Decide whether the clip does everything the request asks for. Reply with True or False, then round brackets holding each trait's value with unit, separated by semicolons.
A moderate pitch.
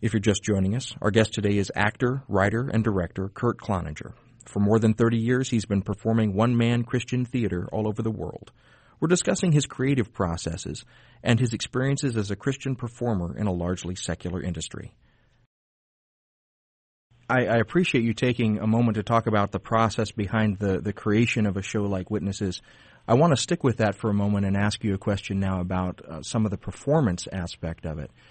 False (110 Hz)